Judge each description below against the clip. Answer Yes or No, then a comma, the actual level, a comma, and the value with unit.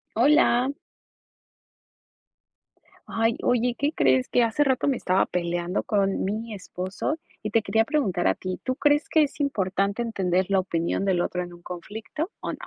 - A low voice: No, high, 210 Hz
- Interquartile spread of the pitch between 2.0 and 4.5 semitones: No, average, 5.3 semitones